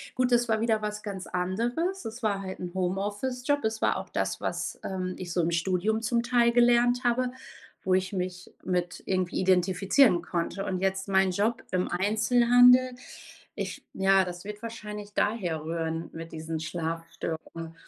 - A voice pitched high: Yes, high, 195 Hz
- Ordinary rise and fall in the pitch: Yes, average, 4.5 semitones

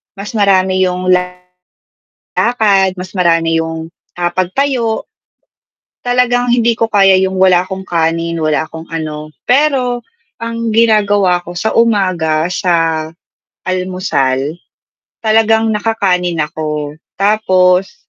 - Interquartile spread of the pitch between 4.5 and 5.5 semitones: Yes, average, 4.8 semitones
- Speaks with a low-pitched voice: No, medium, 185 Hz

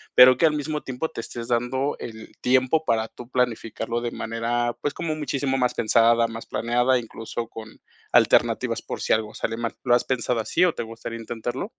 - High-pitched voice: No, low, 120 Hz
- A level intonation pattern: Yes, narrow, 2.3 semitones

